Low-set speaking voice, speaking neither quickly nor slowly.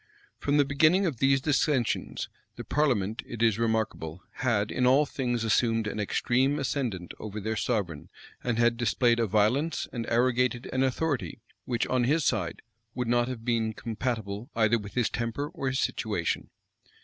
Yes: low, 120 Hz; average, 165 wpm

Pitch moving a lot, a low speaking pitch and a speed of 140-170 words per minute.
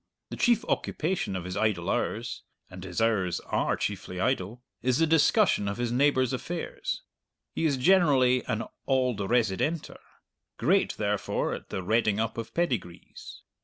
Yes: wide, 6.2 semitones; low, 120 Hz; average, 150 wpm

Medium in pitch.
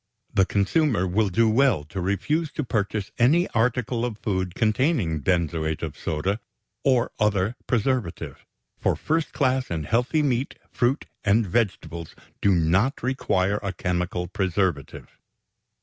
No: low, 105 Hz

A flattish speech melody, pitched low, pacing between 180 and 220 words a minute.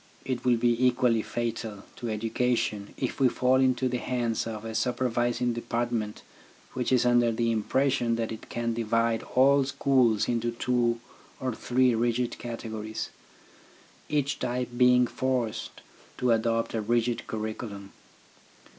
No: narrow, 1.7 semitones; low, 120 Hz; average, 145 wpm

